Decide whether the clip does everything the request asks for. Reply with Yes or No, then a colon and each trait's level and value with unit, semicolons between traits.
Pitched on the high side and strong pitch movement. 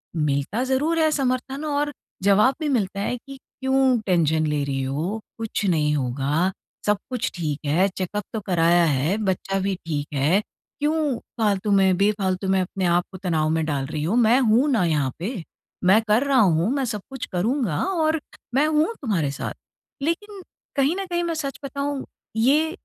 Yes: high, 205 Hz; wide, 8.4 semitones